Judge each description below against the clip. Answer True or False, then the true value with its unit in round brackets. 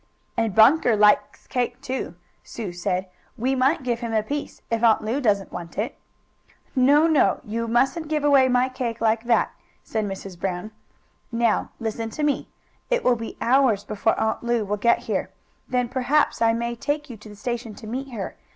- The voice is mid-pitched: False (235 Hz)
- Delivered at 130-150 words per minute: False (190 wpm)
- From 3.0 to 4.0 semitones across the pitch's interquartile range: True (3.3 semitones)